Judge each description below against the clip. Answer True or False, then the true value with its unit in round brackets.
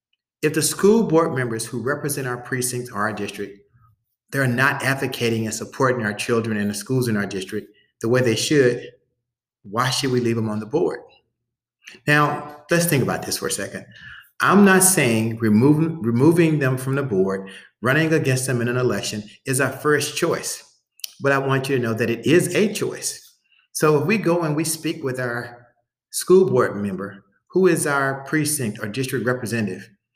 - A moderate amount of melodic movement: True (4.6 semitones)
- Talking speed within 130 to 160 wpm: False (185 wpm)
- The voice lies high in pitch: False (130 Hz)